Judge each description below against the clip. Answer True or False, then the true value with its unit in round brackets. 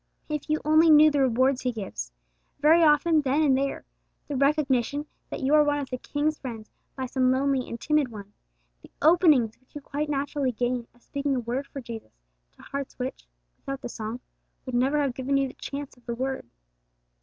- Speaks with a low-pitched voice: False (275 Hz)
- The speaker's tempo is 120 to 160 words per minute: False (200 wpm)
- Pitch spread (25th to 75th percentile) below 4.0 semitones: True (2.9 semitones)